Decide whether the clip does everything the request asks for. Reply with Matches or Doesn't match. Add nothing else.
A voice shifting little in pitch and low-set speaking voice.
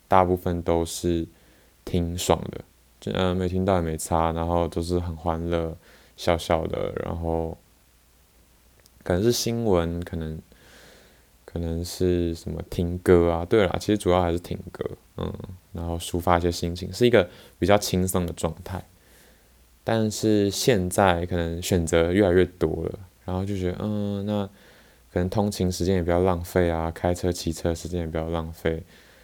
Matches